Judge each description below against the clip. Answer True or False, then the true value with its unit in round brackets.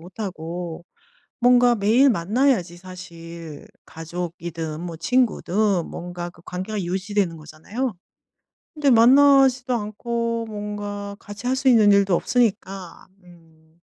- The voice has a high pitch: True (200 Hz)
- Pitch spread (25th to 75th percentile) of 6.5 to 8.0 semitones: False (5.3 semitones)